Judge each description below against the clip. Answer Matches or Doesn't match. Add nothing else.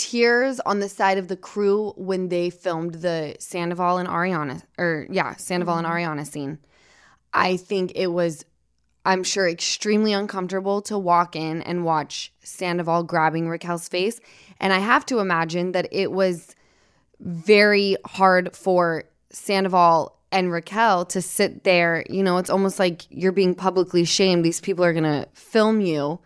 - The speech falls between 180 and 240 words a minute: Doesn't match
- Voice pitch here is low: Doesn't match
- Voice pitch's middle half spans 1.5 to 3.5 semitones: Matches